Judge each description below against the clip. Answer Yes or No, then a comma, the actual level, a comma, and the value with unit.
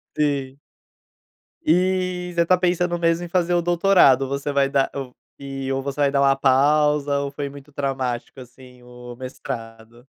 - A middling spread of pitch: Yes, average, 4.2 semitones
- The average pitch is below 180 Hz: Yes, medium, 140 Hz